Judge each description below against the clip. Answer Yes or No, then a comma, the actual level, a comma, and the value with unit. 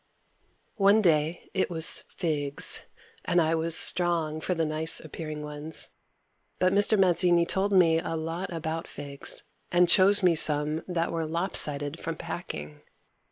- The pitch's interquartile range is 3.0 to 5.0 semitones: No, narrow, 2.4 semitones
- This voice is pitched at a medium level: Yes, medium, 165 Hz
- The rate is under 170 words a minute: Yes, average, 150 wpm